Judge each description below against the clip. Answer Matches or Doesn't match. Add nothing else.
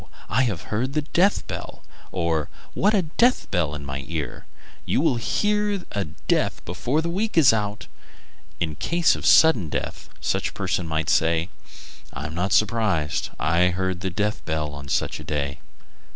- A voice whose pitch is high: Doesn't match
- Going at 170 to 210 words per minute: Matches